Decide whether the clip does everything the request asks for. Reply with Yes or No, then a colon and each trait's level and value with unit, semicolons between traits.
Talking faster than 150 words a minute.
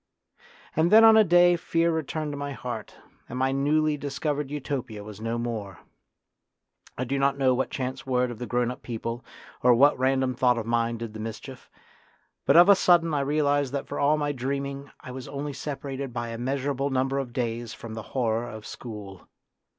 Yes: average, 195 wpm